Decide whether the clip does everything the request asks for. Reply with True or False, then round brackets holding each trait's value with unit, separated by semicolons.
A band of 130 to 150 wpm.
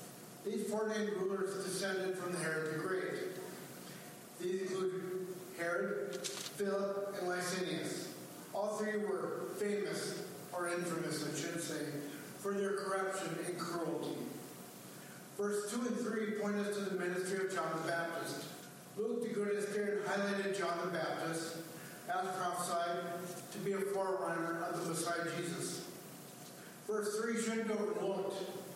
True (135 wpm)